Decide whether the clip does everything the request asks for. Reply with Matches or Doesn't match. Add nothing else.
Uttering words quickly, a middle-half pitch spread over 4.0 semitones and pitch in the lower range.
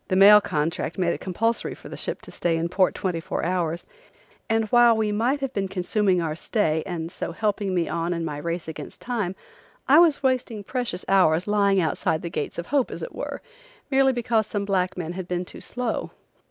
Doesn't match